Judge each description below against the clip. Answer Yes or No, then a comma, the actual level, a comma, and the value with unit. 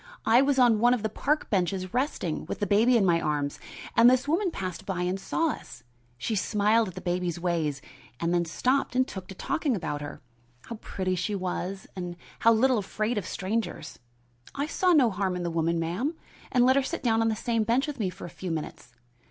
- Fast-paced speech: Yes, fast, 220 wpm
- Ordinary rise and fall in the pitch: No, wide, 5.7 semitones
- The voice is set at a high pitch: Yes, high, 205 Hz